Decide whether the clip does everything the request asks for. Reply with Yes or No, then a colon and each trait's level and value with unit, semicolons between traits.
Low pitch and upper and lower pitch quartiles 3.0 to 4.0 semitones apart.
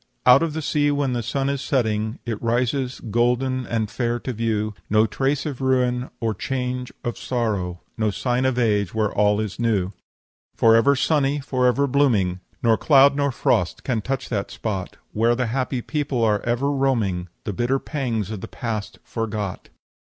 Yes: low, 120 Hz; average, 3.7 semitones